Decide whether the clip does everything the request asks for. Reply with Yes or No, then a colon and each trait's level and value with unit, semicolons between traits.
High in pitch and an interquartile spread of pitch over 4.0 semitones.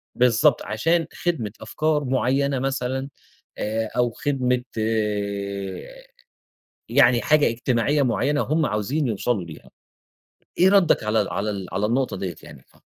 No: low, 125 Hz; average, 4.9 semitones